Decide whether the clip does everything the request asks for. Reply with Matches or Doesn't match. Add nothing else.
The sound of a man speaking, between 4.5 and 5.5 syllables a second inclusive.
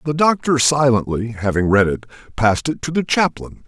Matches